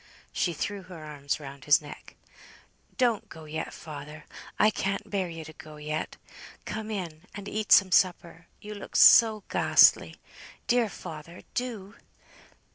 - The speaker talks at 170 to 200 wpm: No, average, 145 wpm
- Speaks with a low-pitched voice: No, medium, 175 Hz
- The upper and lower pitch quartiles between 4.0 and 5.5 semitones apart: Yes, average, 5.1 semitones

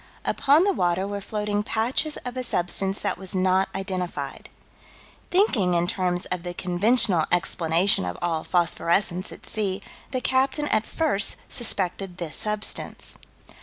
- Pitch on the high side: Yes, high, 195 Hz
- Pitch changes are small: No, average, 4.0 semitones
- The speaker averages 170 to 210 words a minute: No, average, 140 wpm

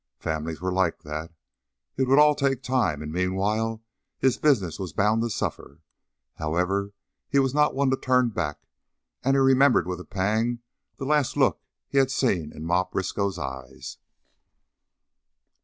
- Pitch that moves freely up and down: Yes, wide, 7.0 semitones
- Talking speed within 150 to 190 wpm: Yes, average, 155 wpm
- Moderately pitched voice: No, low, 105 Hz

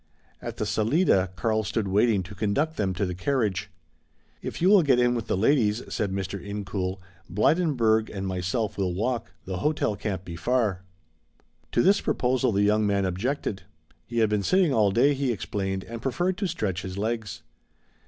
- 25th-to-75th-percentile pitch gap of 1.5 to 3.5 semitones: No, average, 4.3 semitones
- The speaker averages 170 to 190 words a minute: Yes, average, 180 wpm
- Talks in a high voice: No, low, 105 Hz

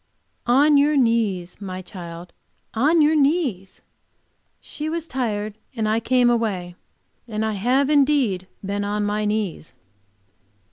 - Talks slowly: Yes, slow, 130 wpm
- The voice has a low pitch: No, high, 220 Hz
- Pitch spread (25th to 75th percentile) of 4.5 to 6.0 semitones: Yes, wide, 5.5 semitones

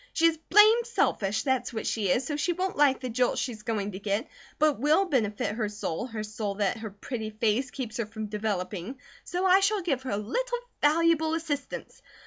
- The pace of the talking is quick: Yes, fast, 210 wpm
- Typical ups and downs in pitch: No, wide, 7.0 semitones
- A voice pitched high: Yes, very high, 250 Hz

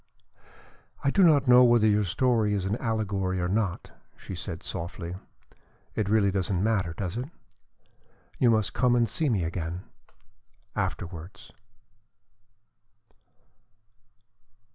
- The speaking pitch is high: No, low, 105 Hz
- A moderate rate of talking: No, slow, 120 wpm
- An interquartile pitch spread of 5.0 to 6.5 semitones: No, average, 4.2 semitones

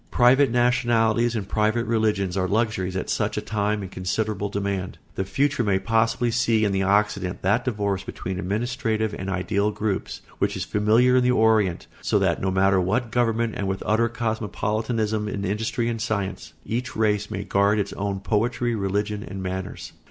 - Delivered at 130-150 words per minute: No, average, 180 wpm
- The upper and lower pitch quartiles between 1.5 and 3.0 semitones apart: Yes, average, 2.7 semitones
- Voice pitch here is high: No, low, 105 Hz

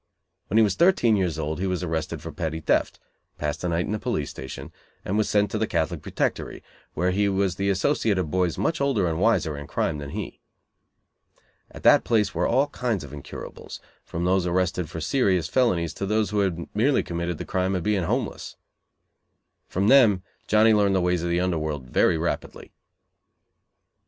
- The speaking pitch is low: Yes, very low, 90 Hz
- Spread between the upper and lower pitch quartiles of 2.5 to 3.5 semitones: No, average, 4.0 semitones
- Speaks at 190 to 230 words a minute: Yes, average, 195 wpm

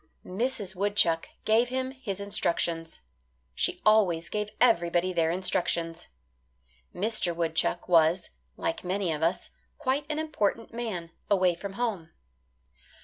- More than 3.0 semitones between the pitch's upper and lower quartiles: Yes, average, 5.0 semitones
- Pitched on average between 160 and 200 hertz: Yes, high, 190 Hz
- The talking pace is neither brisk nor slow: No, slow, 120 wpm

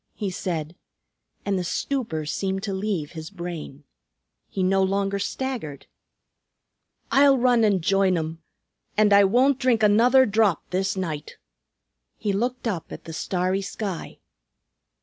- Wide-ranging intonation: No, average, 3.8 semitones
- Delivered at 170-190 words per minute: No, slow, 135 wpm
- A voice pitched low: No, high, 195 Hz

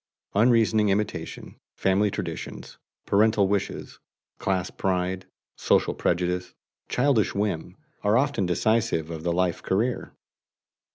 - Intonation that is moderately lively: Yes, average, 3.3 semitones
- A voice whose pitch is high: No, low, 100 Hz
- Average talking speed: No, slow, 105 wpm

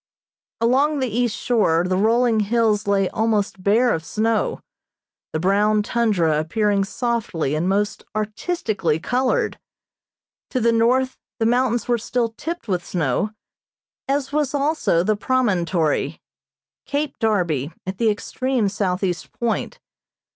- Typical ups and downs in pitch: Yes, average, 4.3 semitones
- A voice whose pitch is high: Yes, high, 215 Hz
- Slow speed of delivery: Yes, slow, 125 wpm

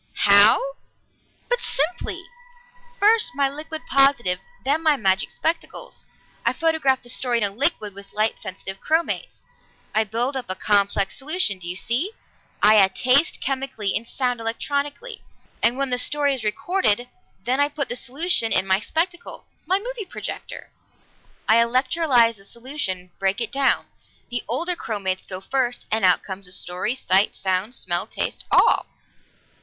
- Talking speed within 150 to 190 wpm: Yes, average, 155 wpm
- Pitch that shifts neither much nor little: No, wide, 6.1 semitones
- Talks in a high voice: Yes, high, 245 Hz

